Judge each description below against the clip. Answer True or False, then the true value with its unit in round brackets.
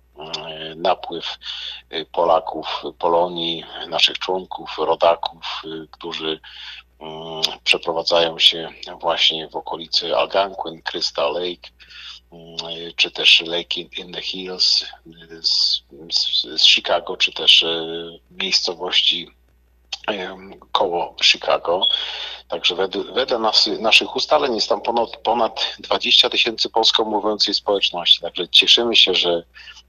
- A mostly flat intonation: True (1.4 semitones)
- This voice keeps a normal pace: False (90 wpm)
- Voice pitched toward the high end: False (85 Hz)